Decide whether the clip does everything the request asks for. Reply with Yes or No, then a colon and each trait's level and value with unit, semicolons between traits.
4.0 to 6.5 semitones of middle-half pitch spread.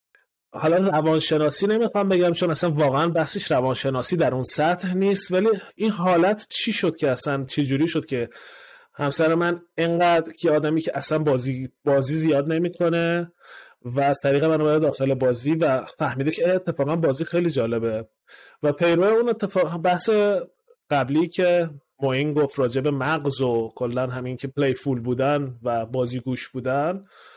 Yes: average, 4.4 semitones